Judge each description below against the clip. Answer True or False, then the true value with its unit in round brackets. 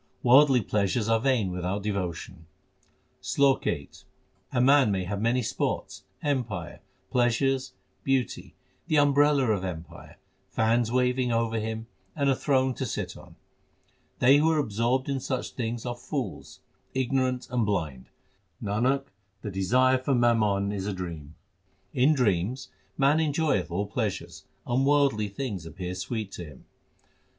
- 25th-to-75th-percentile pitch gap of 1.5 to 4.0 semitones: False (4.9 semitones)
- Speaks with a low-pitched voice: True (120 Hz)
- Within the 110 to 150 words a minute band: True (140 wpm)